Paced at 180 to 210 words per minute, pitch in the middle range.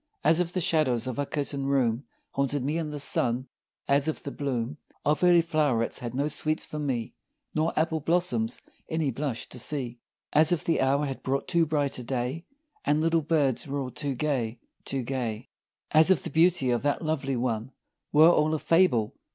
Yes: average, 195 wpm; medium, 145 Hz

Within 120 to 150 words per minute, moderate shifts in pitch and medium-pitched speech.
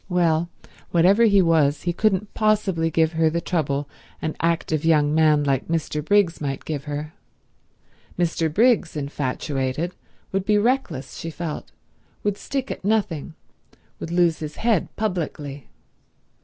Yes: average, 140 wpm; average, 4.2 semitones; medium, 165 Hz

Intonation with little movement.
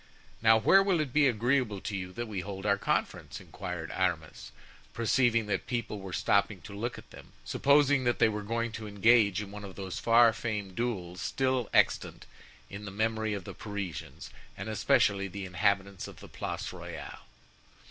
No: average, 3.1 semitones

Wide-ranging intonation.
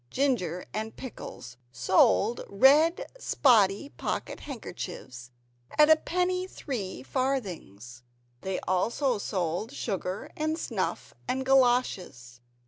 Yes: wide, 7.2 semitones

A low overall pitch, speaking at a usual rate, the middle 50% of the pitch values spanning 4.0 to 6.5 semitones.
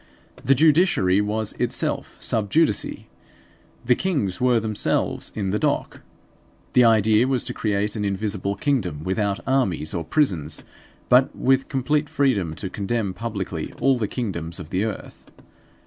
Yes: low, 105 Hz; average, 145 wpm; average, 5.1 semitones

